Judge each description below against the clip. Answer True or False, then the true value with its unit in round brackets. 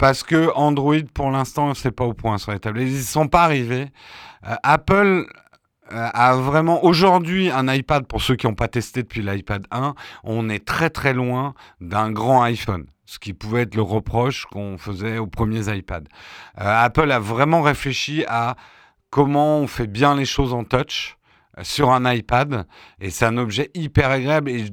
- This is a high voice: False (125 Hz)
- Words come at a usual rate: True (185 wpm)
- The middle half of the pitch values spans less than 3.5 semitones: False (4.4 semitones)